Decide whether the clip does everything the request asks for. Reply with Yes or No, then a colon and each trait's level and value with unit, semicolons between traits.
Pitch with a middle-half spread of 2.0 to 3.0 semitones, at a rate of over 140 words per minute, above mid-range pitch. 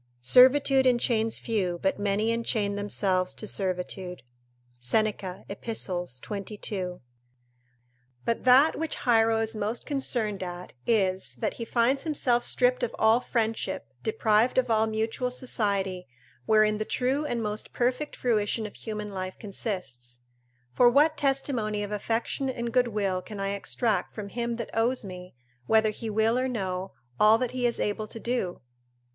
No: average, 3.5 semitones; average, 150 wpm; high, 220 Hz